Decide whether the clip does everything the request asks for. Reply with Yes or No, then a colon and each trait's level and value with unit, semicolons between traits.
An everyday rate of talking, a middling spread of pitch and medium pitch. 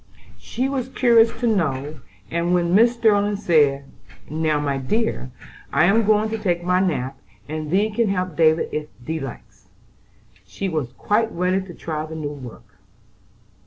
No: average, 160 wpm; wide, 6.0 semitones; medium, 170 Hz